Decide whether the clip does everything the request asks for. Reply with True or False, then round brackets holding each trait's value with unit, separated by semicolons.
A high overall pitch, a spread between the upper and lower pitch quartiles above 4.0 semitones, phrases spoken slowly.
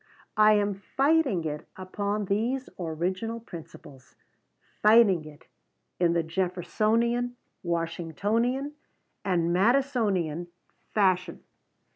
True (195 Hz; 5.1 semitones; 85 wpm)